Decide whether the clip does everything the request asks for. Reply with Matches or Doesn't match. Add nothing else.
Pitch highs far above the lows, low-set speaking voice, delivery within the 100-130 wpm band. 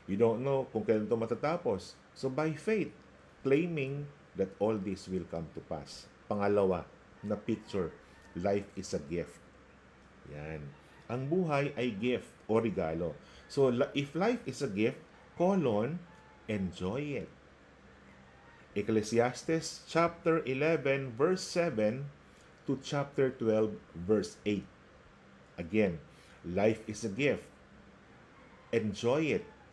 Matches